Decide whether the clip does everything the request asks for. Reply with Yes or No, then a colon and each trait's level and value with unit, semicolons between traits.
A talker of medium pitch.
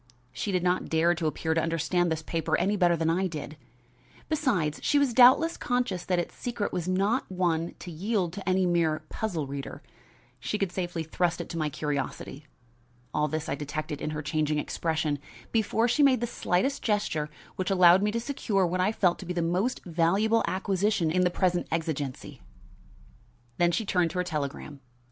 Yes: medium, 175 Hz